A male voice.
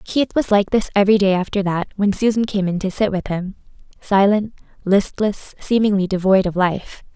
No: female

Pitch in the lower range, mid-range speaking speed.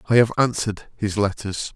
Yes: low, 105 Hz; average, 170 wpm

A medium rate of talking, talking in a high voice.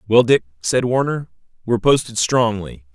No: average, 145 wpm; low, 110 Hz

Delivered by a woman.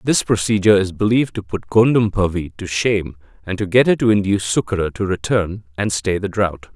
No: male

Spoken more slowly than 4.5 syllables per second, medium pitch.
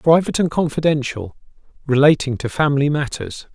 No: 5.7 syllables/s; medium, 145 Hz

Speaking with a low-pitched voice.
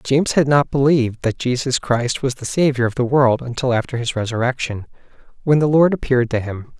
Yes: low, 130 Hz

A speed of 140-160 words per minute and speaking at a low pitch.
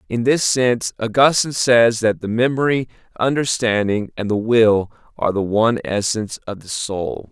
Yes: average, 155 wpm; low, 115 Hz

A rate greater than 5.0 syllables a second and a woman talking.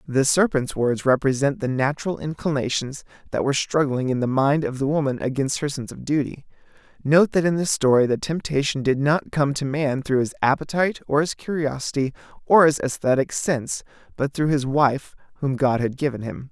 No: 5.5 syllables/s; male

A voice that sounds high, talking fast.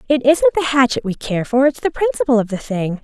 Yes: very high, 255 Hz; fast, 255 wpm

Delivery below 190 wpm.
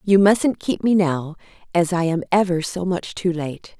No: fast, 205 wpm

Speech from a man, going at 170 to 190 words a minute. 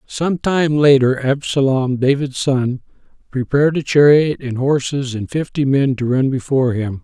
No: male; average, 155 wpm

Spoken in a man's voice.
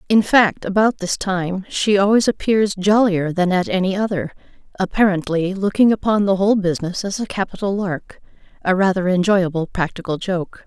No: female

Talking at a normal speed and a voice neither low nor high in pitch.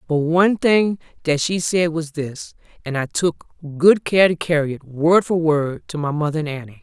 No: fast, 210 wpm; medium, 160 Hz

